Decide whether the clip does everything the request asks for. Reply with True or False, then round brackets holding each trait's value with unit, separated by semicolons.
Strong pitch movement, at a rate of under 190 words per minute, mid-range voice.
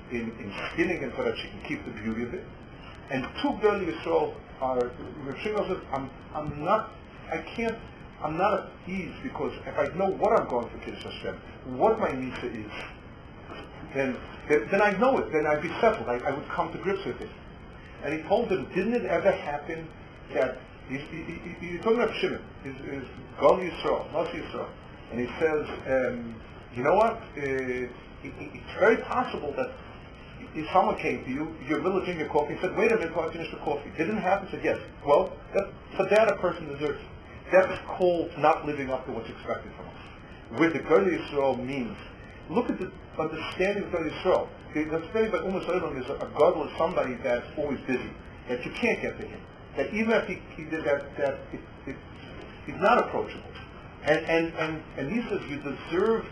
False (6.0 semitones; 195 wpm; 160 Hz)